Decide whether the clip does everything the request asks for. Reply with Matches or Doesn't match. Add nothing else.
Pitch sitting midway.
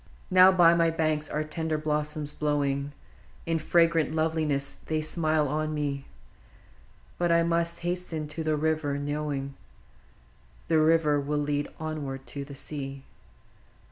Matches